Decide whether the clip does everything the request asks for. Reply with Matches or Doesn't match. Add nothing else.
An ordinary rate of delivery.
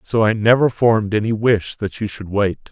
Doesn't match